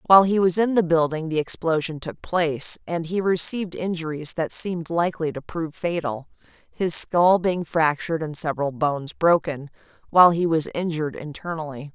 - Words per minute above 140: Yes, average, 165 wpm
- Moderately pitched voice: Yes, medium, 165 Hz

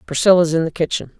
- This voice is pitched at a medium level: Yes, medium, 165 Hz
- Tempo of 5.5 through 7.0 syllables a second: Yes, 6.7 syllables/s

